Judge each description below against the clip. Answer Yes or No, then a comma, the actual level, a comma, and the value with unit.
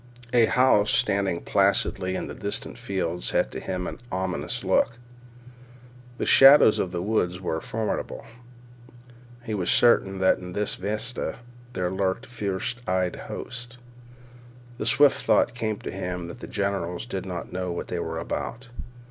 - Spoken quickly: No, average, 150 wpm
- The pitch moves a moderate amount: Yes, average, 3.8 semitones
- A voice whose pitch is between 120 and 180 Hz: No, very low, 95 Hz